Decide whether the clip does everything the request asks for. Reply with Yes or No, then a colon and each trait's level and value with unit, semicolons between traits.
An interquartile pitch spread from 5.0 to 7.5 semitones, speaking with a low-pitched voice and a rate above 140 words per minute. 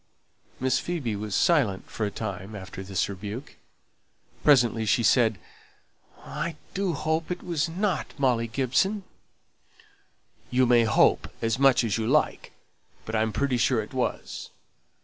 No: wide, 5.6 semitones; low, 125 Hz; slow, 135 wpm